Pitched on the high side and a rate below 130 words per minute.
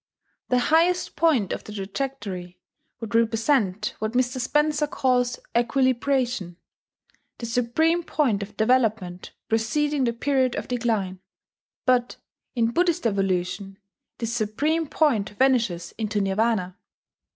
Yes: high, 235 Hz; slow, 115 wpm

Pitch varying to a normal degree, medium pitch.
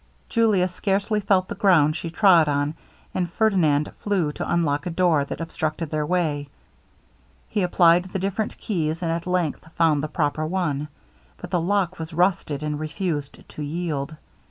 Yes: average, 3.4 semitones; medium, 170 Hz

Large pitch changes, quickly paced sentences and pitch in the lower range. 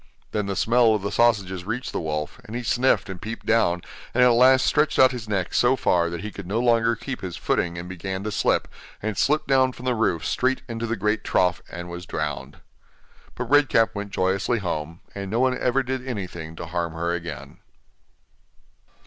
Yes: wide, 5.7 semitones; fast, 210 wpm; low, 105 Hz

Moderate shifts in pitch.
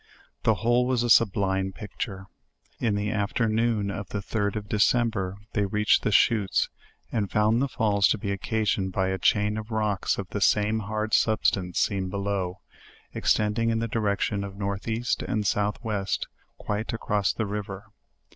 No: narrow, 2.0 semitones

